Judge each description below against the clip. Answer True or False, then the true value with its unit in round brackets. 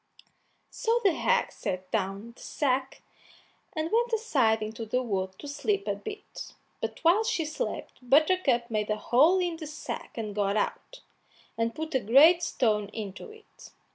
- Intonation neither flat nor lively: False (8.6 semitones)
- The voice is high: True (270 Hz)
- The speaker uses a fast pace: False (165 wpm)